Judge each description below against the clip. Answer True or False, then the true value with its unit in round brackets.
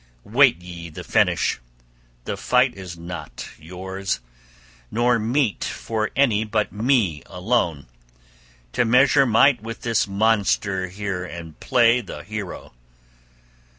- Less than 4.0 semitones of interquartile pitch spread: False (4.7 semitones)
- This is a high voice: False (105 Hz)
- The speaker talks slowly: True (120 wpm)